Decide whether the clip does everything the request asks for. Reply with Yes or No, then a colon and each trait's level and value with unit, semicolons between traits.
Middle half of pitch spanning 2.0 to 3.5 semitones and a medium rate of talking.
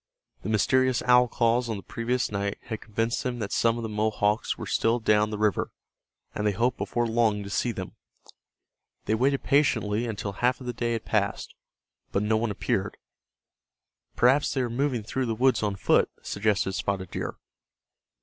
Yes: average, 2.8 semitones; average, 180 wpm